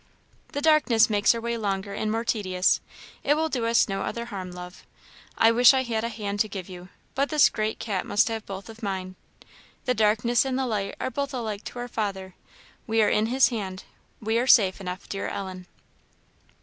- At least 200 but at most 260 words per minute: Yes, fast, 205 wpm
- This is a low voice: No, high, 220 Hz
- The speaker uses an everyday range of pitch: Yes, average, 3.3 semitones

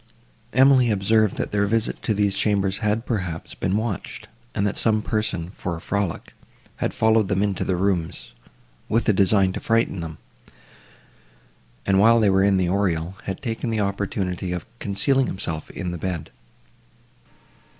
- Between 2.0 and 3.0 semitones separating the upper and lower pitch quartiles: Yes, average, 2.7 semitones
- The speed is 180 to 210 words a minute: No, average, 160 wpm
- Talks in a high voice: No, low, 100 Hz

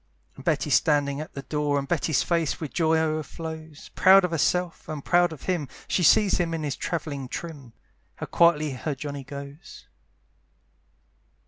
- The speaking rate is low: No, average, 160 wpm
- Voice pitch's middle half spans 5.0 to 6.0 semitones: No, average, 2.9 semitones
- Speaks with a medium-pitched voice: Yes, medium, 155 Hz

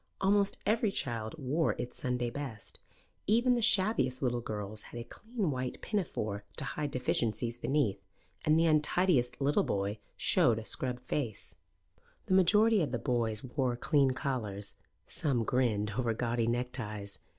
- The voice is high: No, low, 125 Hz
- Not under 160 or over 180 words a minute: No, average, 150 wpm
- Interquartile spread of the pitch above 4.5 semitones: Yes, average, 5.1 semitones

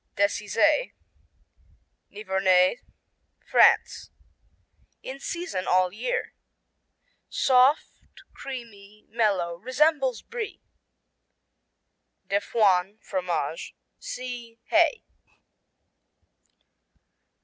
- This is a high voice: Yes, high, 225 Hz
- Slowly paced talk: Yes, slow, 60 wpm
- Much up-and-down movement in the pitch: Yes, wide, 6.1 semitones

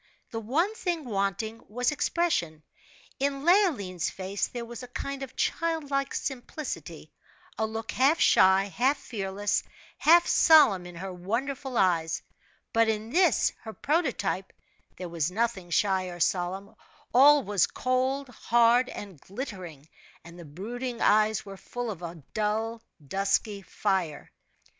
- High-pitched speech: Yes, high, 220 Hz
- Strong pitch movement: Yes, wide, 5.8 semitones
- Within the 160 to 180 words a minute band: No, slow, 135 wpm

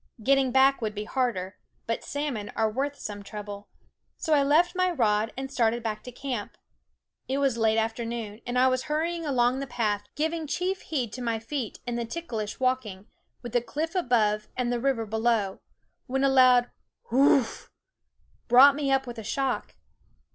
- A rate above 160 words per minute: Yes, average, 190 wpm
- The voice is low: No, high, 245 Hz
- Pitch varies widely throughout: No, average, 3.8 semitones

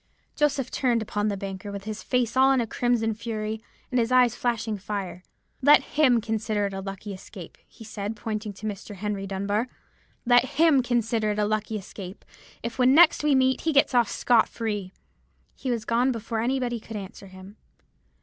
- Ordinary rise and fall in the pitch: Yes, average, 3.2 semitones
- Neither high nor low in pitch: No, high, 220 Hz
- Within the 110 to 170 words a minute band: No, average, 190 wpm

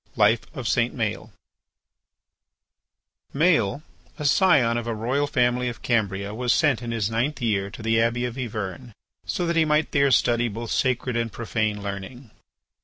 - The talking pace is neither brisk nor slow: Yes, average, 165 wpm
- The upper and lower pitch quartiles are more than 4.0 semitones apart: No, average, 3.4 semitones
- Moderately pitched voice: No, low, 120 Hz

